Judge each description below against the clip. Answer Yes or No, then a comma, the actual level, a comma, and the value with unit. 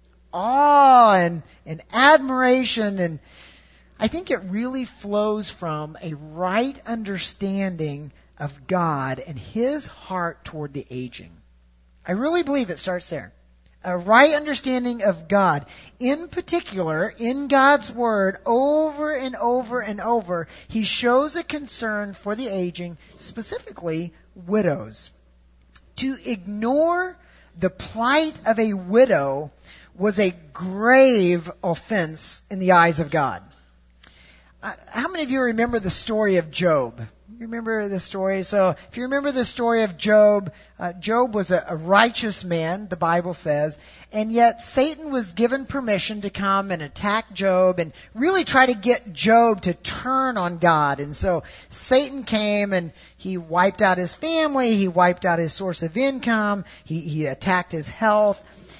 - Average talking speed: Yes, average, 145 wpm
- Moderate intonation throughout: No, wide, 6.4 semitones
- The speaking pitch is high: Yes, high, 200 Hz